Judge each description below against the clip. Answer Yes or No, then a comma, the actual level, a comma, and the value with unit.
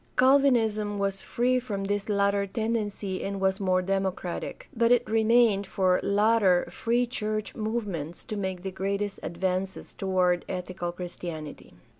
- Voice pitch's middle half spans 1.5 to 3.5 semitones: Yes, average, 2.9 semitones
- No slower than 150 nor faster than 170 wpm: No, slow, 135 wpm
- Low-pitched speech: No, high, 200 Hz